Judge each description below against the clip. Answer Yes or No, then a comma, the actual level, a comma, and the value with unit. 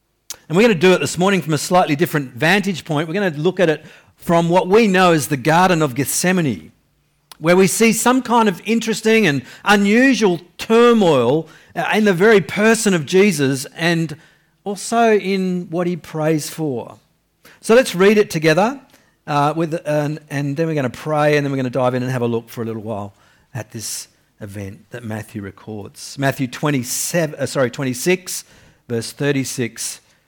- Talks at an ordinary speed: Yes, average, 185 wpm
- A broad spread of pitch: Yes, wide, 6.1 semitones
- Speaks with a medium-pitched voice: Yes, medium, 160 Hz